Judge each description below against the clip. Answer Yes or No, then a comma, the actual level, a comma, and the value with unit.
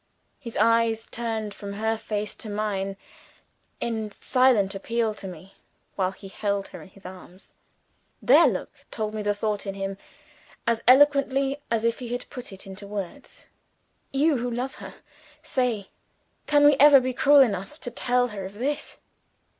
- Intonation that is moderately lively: Yes, average, 3.9 semitones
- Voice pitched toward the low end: No, high, 220 Hz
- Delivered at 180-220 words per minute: No, average, 165 wpm